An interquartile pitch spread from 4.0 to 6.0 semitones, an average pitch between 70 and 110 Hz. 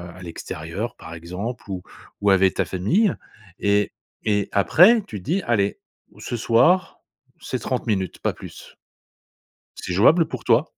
Yes: average, 5.2 semitones; low, 105 Hz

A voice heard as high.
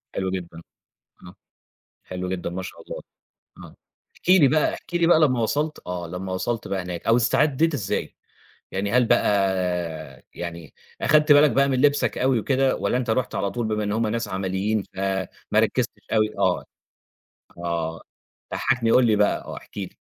No: low, 110 Hz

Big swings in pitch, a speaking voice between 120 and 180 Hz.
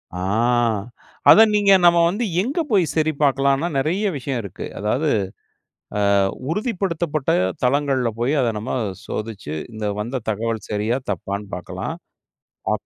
Yes: wide, 7.3 semitones; low, 135 Hz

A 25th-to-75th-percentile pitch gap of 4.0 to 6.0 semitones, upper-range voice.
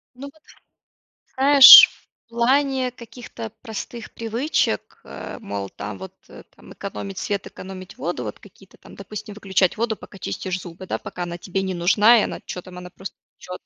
Yes: average, 4.6 semitones; high, 195 Hz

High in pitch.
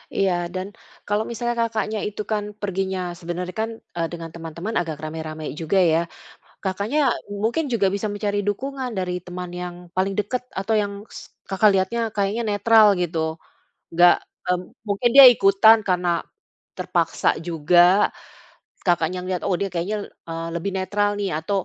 Yes: high, 195 Hz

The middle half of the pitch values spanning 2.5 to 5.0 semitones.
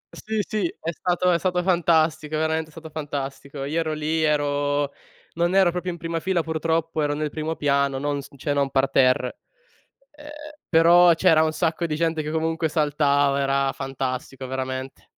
Yes: average, 2.8 semitones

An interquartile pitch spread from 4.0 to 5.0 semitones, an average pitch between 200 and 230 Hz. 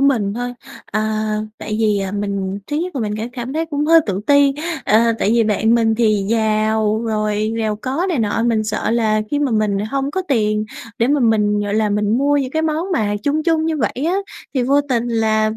Yes: average, 4.6 semitones; high, 225 Hz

